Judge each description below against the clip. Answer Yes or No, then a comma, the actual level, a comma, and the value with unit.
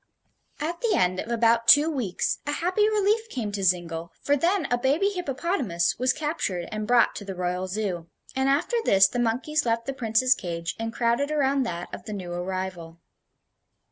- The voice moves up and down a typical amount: No, wide, 7.7 semitones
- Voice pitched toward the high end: Yes, high, 235 Hz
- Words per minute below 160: No, average, 185 wpm